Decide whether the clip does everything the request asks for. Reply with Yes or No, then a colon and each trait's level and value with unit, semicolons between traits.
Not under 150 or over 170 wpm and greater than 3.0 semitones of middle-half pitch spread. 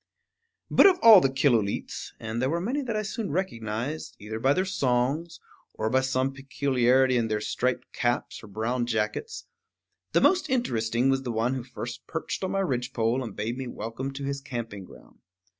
No: average, 185 wpm; average, 3.9 semitones